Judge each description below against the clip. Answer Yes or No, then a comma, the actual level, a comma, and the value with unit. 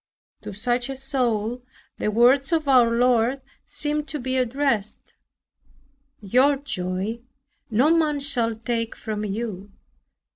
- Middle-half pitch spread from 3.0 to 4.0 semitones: Yes, average, 3.7 semitones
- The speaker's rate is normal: No, slow, 120 wpm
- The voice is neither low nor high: No, high, 245 Hz